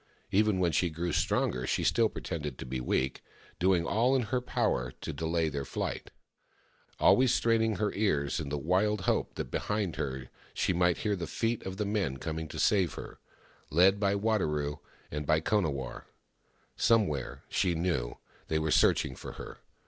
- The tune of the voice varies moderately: No, wide, 5.9 semitones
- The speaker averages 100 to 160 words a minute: No, average, 175 wpm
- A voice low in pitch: Yes, very low, 85 Hz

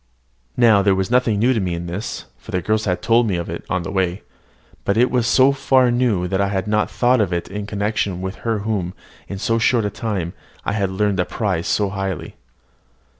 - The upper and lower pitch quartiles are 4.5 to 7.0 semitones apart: No, average, 3.3 semitones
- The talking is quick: Yes, fast, 225 wpm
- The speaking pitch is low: Yes, low, 100 Hz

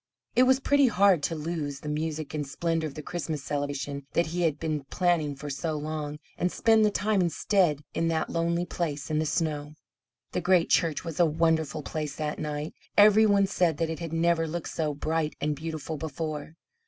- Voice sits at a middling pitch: Yes, medium, 160 Hz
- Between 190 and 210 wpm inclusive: Yes, average, 200 wpm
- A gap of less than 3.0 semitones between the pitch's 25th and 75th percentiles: Yes, narrow, 2.4 semitones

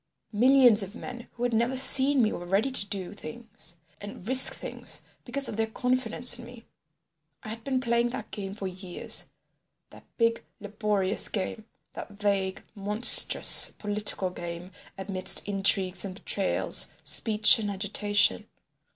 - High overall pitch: Yes, high, 210 Hz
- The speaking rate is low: No, average, 145 wpm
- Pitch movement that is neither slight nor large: Yes, average, 3.5 semitones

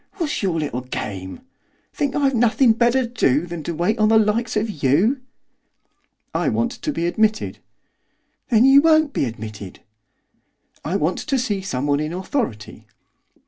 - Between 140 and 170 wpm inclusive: Yes, average, 155 wpm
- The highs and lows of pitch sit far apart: Yes, wide, 8.6 semitones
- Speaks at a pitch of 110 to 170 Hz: No, high, 210 Hz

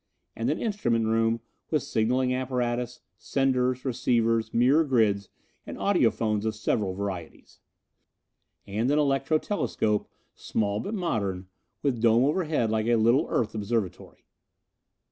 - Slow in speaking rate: Yes, slow, 125 wpm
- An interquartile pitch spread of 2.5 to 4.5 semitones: Yes, average, 3.3 semitones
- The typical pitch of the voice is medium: No, low, 115 Hz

